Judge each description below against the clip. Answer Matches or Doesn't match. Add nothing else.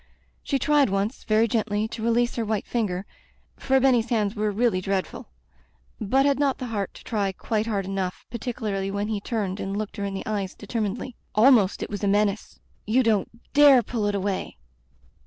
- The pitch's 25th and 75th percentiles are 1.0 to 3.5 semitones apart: Matches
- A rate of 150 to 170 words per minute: Doesn't match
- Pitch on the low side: Doesn't match